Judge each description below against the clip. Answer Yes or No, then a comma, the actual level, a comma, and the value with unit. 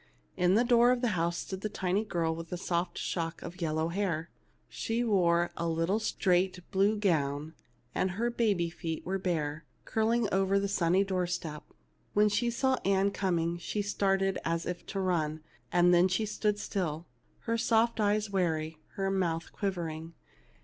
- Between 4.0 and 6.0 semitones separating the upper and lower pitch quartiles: No, average, 3.5 semitones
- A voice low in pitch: No, medium, 185 Hz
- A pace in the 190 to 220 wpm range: No, average, 170 wpm